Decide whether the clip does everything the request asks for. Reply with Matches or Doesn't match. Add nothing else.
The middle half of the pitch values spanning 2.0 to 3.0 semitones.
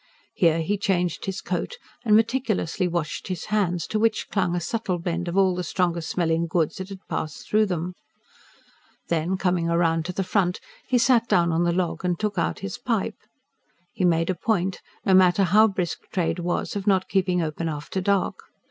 Matches